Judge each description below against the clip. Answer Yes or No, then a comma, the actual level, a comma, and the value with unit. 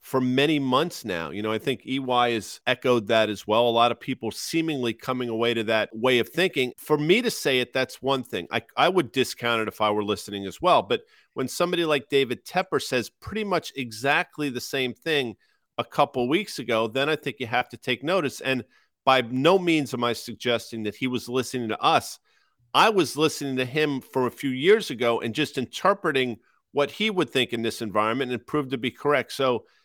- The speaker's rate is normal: No, fast, 220 wpm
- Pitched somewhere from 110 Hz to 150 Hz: Yes, low, 130 Hz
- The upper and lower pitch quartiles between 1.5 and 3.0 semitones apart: No, average, 4.2 semitones